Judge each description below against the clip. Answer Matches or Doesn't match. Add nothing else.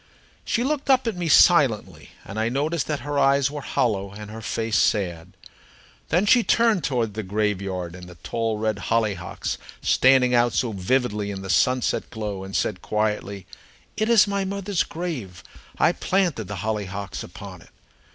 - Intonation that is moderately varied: Doesn't match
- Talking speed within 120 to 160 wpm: Doesn't match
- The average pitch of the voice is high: Doesn't match